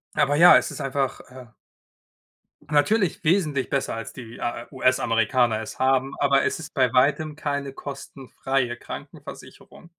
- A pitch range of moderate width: No, narrow, 2.3 semitones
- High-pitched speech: No, low, 135 Hz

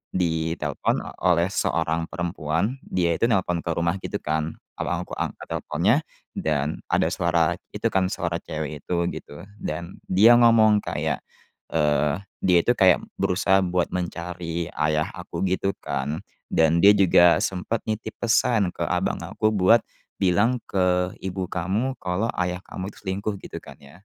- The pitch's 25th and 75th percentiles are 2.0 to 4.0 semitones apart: Yes, average, 2.9 semitones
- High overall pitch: No, very low, 90 Hz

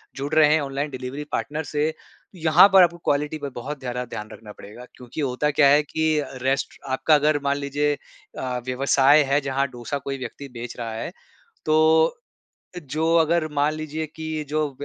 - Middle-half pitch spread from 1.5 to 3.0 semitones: Yes, average, 2.7 semitones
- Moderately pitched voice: Yes, medium, 145 Hz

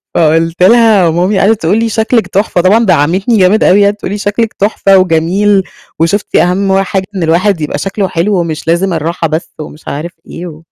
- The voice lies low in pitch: No, medium, 185 Hz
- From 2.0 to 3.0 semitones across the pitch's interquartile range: No, average, 3.6 semitones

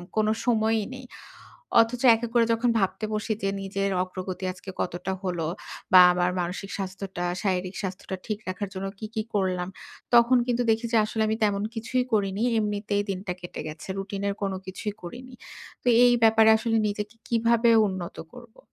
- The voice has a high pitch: Yes, high, 205 Hz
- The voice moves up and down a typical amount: Yes, average, 3.1 semitones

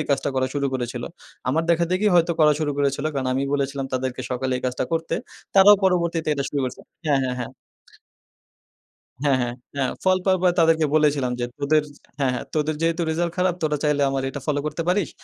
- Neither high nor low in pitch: Yes, medium, 150 Hz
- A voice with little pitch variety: No, average, 3.7 semitones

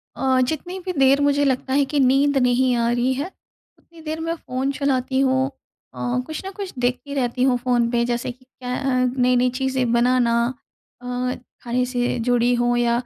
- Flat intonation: Yes, narrow, 2.1 semitones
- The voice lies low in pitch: No, very high, 255 Hz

